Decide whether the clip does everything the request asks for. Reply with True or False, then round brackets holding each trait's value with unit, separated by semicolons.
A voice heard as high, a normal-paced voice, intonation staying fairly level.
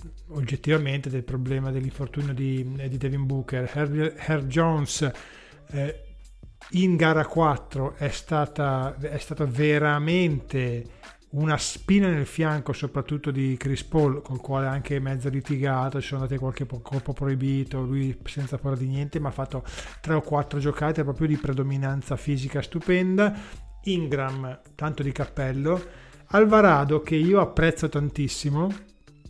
False (140 Hz; 135 wpm; 2.3 semitones)